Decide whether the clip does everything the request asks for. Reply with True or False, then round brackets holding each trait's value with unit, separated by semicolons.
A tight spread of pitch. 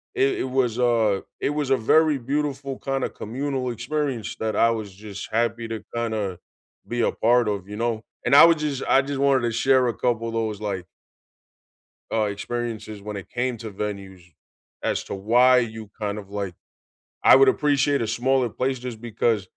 False (3.8 semitones)